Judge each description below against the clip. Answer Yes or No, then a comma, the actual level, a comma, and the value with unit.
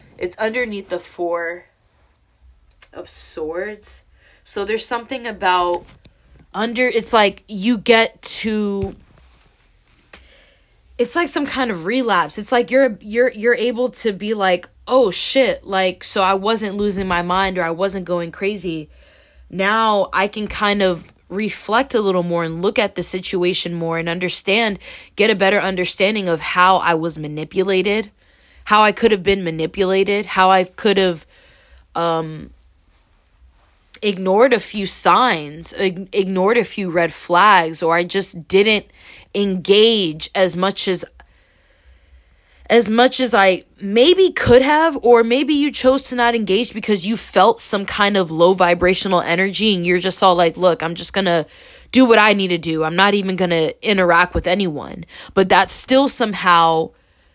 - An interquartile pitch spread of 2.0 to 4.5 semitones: Yes, average, 4.0 semitones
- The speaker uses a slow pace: No, average, 155 wpm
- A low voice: No, high, 195 Hz